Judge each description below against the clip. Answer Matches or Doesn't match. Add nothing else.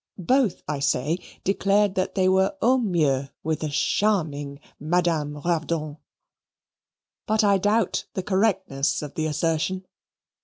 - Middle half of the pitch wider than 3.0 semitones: Matches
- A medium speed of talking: Doesn't match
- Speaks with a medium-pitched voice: Matches